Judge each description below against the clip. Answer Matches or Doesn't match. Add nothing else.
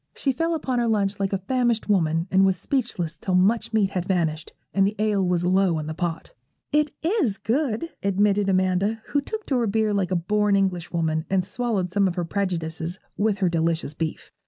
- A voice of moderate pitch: Doesn't match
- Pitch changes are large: Doesn't match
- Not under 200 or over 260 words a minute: Matches